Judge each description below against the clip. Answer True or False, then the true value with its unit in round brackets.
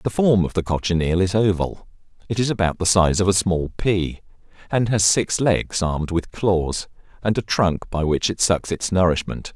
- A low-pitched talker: True (95 Hz)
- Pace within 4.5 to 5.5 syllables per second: True (4.7 syllables/s)